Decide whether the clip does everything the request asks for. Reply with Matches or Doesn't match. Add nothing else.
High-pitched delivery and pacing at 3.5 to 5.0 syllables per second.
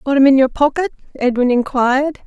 Doesn't match